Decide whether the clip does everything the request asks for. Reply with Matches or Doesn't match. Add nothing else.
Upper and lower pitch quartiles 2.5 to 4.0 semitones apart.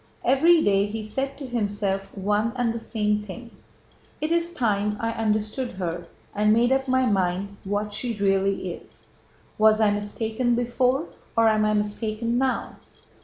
Matches